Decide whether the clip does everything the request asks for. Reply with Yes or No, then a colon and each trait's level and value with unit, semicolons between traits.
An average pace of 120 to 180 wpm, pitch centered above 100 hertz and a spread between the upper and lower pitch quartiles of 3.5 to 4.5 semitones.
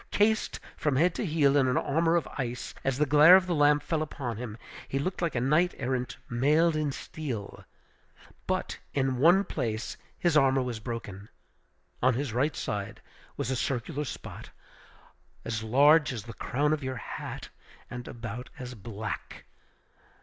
Yes: average, 165 wpm; low, 135 Hz; average, 4.2 semitones